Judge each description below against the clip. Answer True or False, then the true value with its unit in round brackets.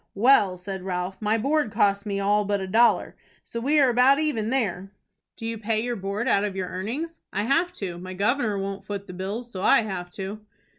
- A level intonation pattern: False (3.7 semitones)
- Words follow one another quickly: True (215 wpm)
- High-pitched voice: True (205 Hz)